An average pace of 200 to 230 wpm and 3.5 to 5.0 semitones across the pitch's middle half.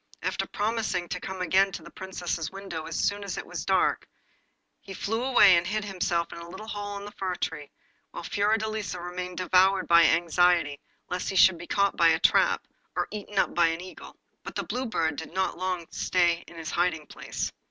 No: fast, 205 wpm; average, 2.8 semitones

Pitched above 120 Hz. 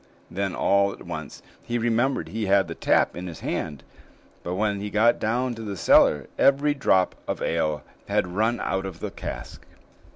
No: low, 100 Hz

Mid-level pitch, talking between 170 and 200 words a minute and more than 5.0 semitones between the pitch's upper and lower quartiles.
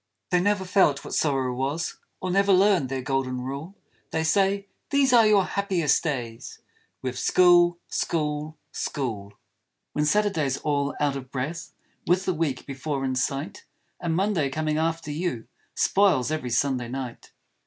No: medium, 155 Hz; average, 155 wpm; wide, 5.4 semitones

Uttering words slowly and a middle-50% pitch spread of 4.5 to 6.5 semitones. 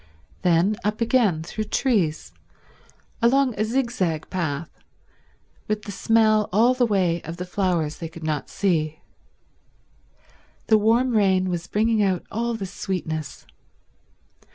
Yes: slow, 130 wpm; average, 4.9 semitones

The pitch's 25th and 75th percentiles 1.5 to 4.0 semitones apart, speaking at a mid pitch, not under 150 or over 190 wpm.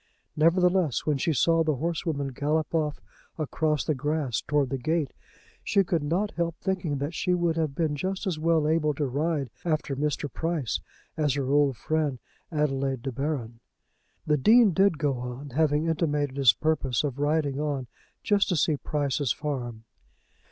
Yes: average, 2.9 semitones; medium, 150 Hz; average, 165 wpm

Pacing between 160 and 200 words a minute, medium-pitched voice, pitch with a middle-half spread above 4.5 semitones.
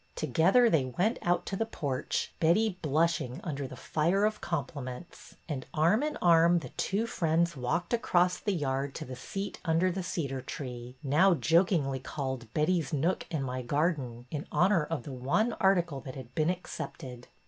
Yes: average, 170 wpm; medium, 160 Hz; average, 5.2 semitones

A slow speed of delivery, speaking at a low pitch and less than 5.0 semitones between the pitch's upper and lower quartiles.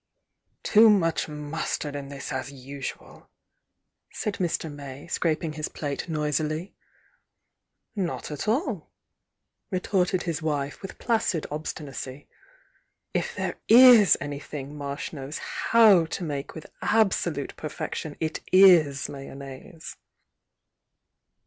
No: slow, 110 wpm; medium, 155 Hz; average, 4.3 semitones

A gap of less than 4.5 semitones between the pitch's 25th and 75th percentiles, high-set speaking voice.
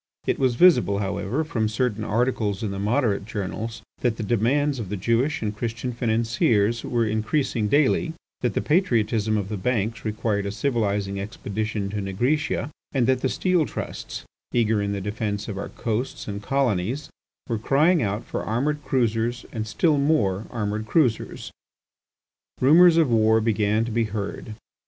No: average, 3.6 semitones; low, 115 Hz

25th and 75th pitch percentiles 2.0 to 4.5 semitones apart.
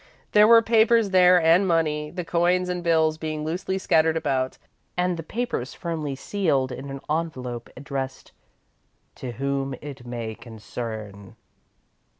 No: average, 5.2 semitones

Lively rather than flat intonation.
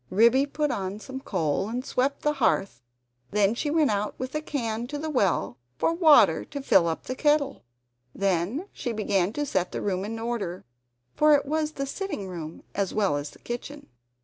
Yes: wide, 6.8 semitones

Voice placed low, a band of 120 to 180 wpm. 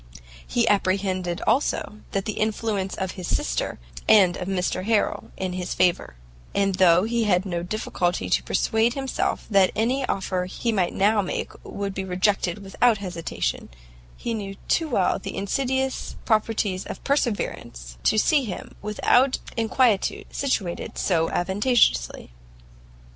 No: high, 200 Hz; slow, 135 wpm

